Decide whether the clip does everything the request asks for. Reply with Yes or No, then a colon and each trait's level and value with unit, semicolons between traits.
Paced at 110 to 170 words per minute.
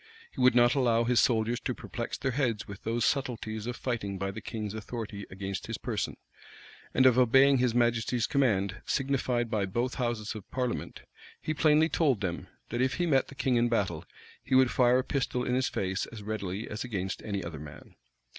No: average, 200 wpm